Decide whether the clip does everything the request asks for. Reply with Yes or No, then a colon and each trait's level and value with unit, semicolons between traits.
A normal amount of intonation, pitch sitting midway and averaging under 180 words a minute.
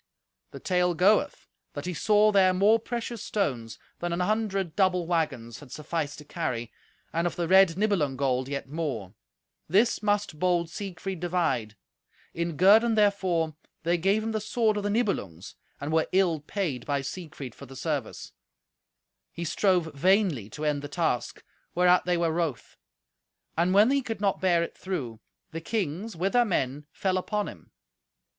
Yes: average, 5.0 semitones; medium, 175 Hz; average, 165 wpm